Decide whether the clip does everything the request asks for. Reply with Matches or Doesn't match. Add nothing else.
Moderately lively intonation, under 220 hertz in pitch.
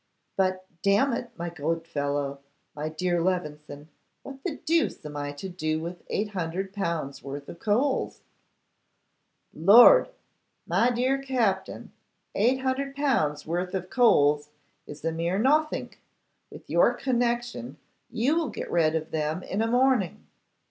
Doesn't match